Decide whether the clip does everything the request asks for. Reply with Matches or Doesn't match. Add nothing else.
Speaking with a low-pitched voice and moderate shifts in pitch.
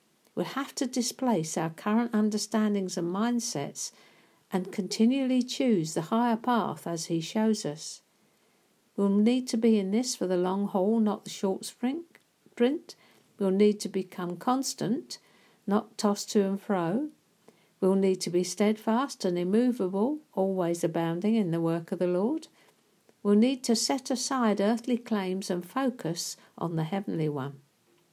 Doesn't match